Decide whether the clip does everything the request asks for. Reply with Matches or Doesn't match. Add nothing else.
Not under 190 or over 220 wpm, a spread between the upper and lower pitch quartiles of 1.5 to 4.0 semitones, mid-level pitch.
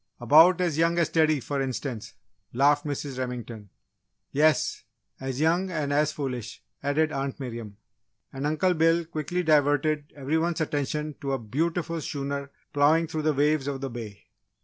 Doesn't match